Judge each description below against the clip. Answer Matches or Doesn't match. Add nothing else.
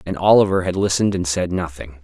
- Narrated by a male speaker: Matches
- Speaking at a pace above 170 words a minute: Matches